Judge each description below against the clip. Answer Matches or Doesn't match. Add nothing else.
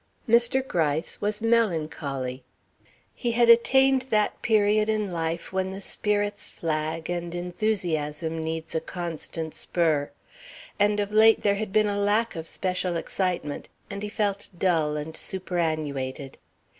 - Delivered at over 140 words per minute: Doesn't match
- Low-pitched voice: Doesn't match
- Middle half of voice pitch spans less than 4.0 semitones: Doesn't match